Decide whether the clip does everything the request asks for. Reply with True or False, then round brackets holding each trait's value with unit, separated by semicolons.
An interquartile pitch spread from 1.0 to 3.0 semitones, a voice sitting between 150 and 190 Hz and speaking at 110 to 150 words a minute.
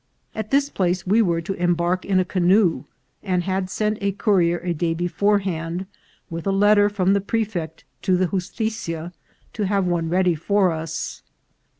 False (2.7 semitones; 185 Hz; 170 wpm)